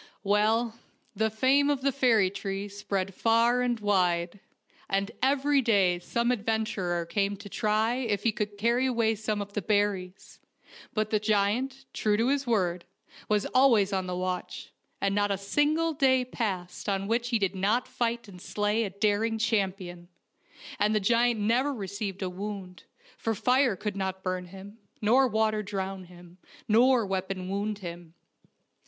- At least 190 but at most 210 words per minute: No, average, 160 wpm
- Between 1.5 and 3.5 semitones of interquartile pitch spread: Yes, average, 3.2 semitones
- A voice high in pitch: Yes, high, 210 Hz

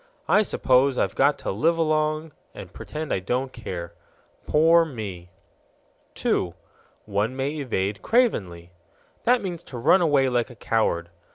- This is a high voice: No, low, 130 Hz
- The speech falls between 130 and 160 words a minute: Yes, average, 145 wpm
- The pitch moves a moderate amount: No, wide, 7.5 semitones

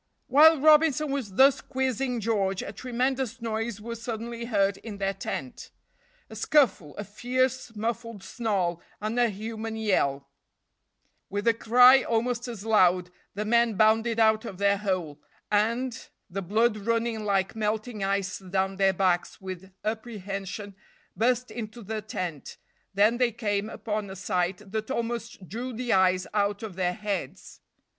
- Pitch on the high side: Yes, high, 215 Hz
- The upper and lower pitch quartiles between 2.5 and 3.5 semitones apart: Yes, average, 3.2 semitones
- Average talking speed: Yes, average, 150 wpm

